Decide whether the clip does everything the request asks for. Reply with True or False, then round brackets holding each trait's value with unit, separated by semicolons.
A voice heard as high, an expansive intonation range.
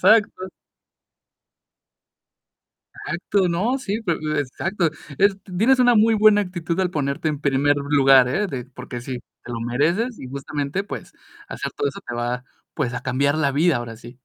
False (150 Hz; 7.0 semitones)